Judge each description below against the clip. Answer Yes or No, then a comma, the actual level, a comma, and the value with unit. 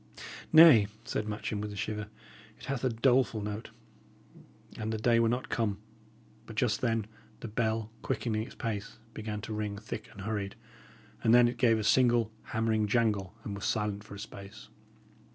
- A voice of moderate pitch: No, low, 110 Hz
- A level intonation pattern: Yes, narrow, 1.9 semitones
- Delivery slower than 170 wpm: No, average, 175 wpm